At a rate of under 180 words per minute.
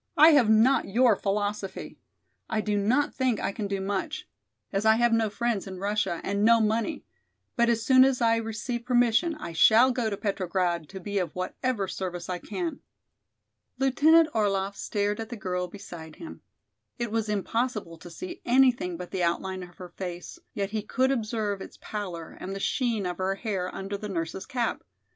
No: average, 185 wpm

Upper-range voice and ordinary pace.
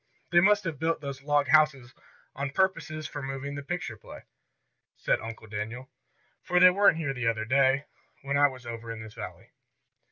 No: medium, 140 Hz; average, 185 wpm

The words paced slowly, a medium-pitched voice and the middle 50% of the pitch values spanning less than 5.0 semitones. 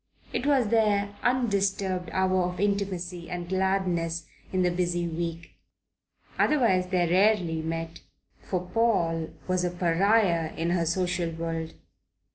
Yes: slow, 125 wpm; medium, 180 Hz; average, 2.8 semitones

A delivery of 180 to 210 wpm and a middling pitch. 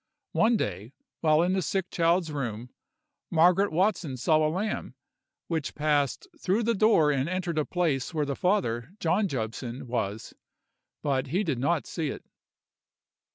No: average, 155 wpm; medium, 155 Hz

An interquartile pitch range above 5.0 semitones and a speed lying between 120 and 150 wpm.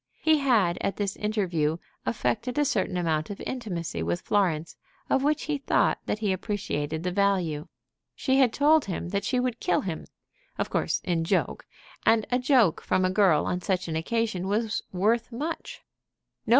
No: wide, 5.4 semitones; average, 175 wpm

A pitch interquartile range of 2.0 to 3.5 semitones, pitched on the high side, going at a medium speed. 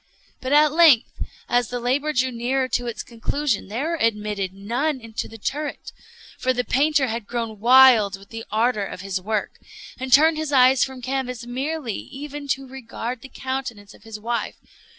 Yes: average, 3.1 semitones; very high, 250 Hz; average, 180 wpm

